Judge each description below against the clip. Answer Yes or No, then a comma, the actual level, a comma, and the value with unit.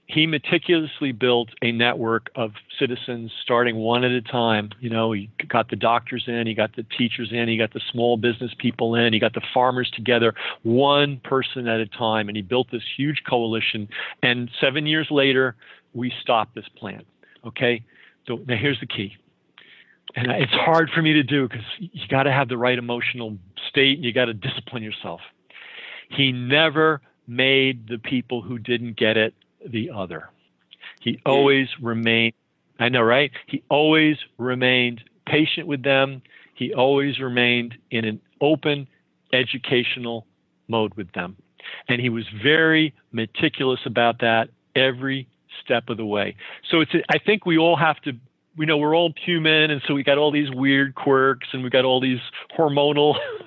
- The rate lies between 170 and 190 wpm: Yes, average, 175 wpm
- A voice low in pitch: Yes, low, 125 Hz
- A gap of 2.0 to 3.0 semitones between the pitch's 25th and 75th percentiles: No, average, 3.4 semitones